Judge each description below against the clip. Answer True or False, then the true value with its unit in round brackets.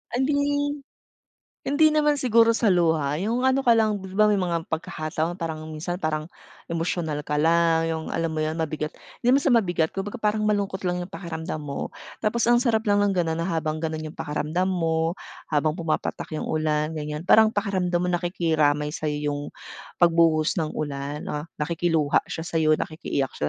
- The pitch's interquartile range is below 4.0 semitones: False (4.7 semitones)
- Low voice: False (165 Hz)